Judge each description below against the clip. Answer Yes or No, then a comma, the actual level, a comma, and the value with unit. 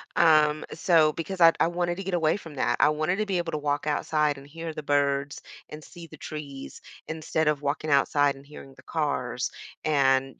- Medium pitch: Yes, medium, 150 Hz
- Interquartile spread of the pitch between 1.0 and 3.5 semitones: Yes, narrow, 2.6 semitones